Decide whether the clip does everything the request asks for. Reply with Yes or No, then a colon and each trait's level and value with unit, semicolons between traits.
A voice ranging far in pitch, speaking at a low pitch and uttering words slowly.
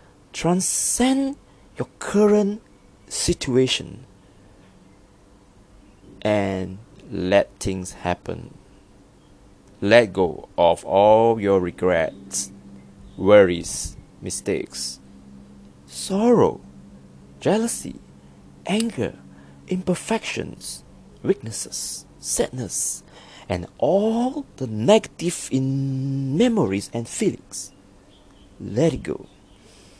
Yes: wide, 7.1 semitones; low, 100 Hz; slow, 65 wpm